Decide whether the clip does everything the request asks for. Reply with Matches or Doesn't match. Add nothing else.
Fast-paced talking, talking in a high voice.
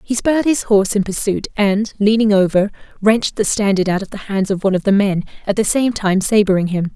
Matches